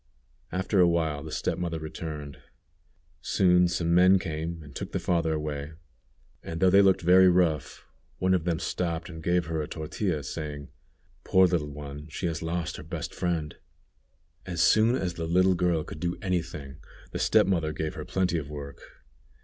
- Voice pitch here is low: Yes, very low, 85 Hz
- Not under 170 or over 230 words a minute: Yes, average, 185 wpm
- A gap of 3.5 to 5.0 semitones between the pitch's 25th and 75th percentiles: No, average, 2.7 semitones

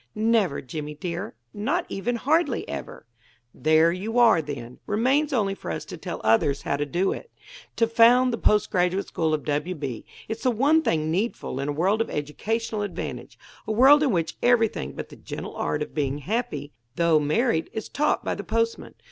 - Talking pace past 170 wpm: Yes, average, 190 wpm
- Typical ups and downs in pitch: No, wide, 7.4 semitones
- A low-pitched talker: No, high, 195 Hz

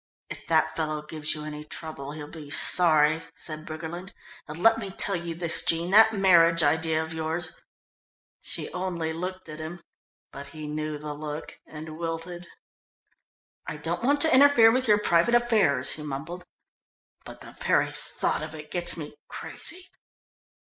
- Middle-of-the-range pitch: Yes, medium, 160 Hz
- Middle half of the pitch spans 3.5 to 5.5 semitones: No, average, 2.8 semitones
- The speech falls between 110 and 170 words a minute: Yes, average, 165 wpm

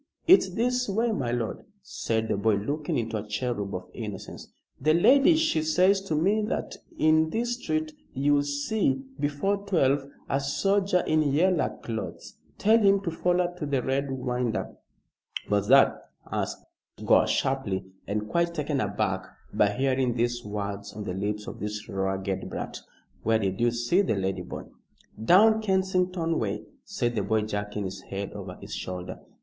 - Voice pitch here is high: No, low, 135 Hz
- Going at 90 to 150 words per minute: No, average, 165 wpm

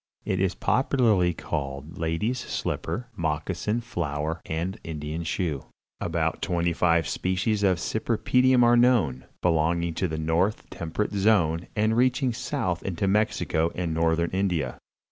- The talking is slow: Yes, slow, 130 wpm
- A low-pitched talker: Yes, very low, 90 Hz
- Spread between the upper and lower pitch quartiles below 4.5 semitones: No, average, 4.8 semitones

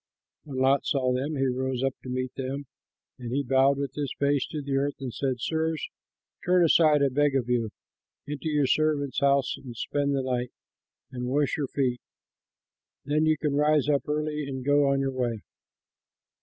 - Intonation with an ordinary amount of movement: No, narrow, 2.2 semitones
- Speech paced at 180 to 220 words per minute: Yes, average, 185 wpm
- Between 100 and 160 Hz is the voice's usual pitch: Yes, medium, 140 Hz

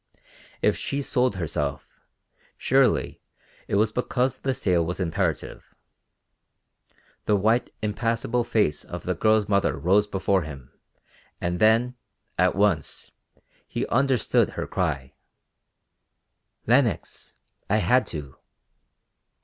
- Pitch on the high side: No, low, 105 Hz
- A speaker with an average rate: No, slow, 110 wpm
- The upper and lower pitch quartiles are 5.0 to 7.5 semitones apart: Yes, average, 5.3 semitones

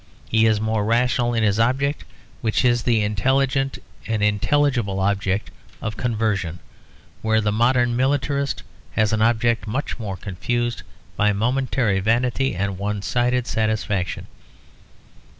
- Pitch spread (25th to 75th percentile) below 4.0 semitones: Yes, average, 3.1 semitones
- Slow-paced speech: Yes, slow, 130 wpm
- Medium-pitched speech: No, low, 115 Hz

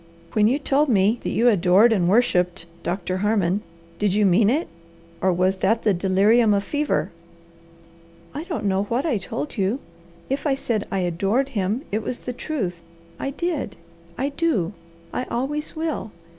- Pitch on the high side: Yes, high, 215 Hz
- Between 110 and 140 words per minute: No, average, 170 wpm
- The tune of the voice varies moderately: No, wide, 6.0 semitones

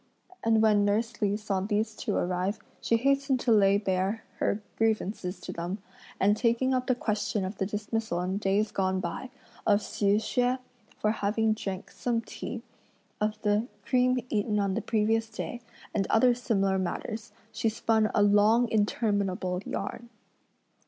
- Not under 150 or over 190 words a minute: Yes, average, 160 wpm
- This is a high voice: Yes, high, 215 Hz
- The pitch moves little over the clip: Yes, narrow, 2.3 semitones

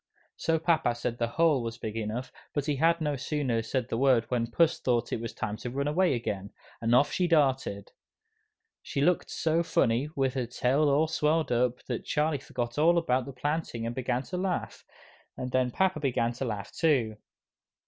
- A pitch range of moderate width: Yes, average, 4.4 semitones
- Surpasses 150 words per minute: Yes, average, 195 wpm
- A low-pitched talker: Yes, low, 130 Hz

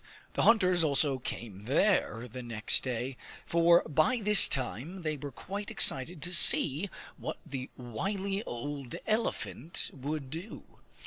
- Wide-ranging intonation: Yes, wide, 6.3 semitones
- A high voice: No, medium, 150 Hz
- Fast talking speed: No, slow, 135 wpm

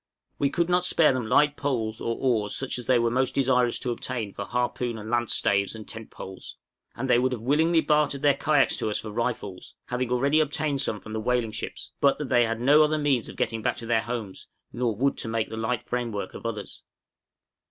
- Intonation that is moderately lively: Yes, average, 3.7 semitones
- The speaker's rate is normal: No, fast, 225 wpm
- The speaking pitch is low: Yes, low, 125 Hz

